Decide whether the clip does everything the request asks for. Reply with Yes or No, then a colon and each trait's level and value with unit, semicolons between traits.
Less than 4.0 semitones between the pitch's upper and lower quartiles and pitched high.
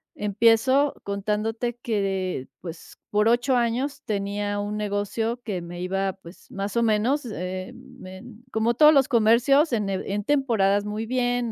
Yes: average, 3.5 semitones; high, 215 Hz